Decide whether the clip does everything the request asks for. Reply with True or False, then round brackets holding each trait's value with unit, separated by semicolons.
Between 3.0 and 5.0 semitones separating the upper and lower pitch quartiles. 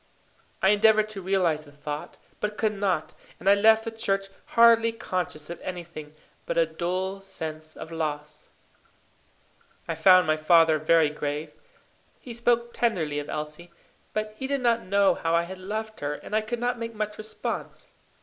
False (5.5 semitones)